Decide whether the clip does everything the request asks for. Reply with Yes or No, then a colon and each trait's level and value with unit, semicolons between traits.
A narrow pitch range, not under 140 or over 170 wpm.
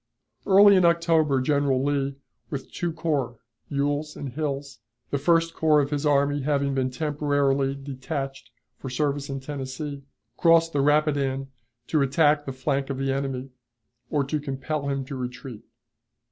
Yes: narrow, 1.9 semitones; average, 150 wpm